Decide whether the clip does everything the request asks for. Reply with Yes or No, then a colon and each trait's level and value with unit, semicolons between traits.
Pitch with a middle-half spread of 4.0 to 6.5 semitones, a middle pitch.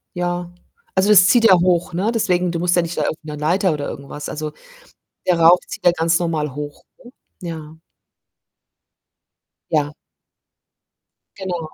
No: average, 2.7 semitones; medium, 170 Hz